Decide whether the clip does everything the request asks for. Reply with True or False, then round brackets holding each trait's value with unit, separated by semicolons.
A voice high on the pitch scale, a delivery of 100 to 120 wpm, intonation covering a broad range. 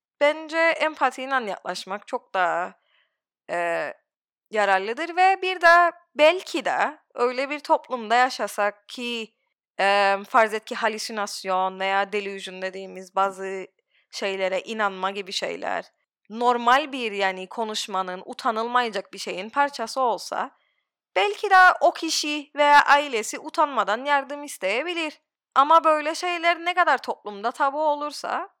True (245 Hz; 115 wpm; 7.2 semitones)